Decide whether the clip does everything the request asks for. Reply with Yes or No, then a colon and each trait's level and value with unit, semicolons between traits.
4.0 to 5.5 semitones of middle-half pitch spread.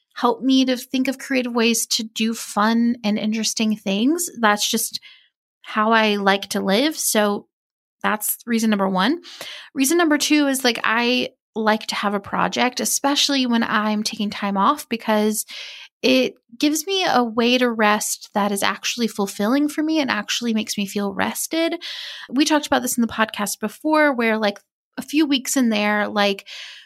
Yes: average, 4.4 semitones